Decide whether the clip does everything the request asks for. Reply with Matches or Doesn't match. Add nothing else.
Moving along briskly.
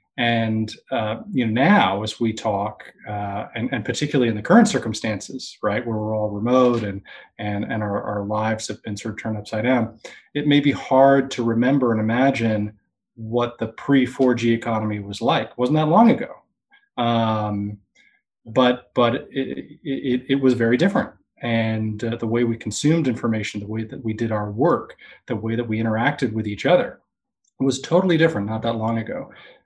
Doesn't match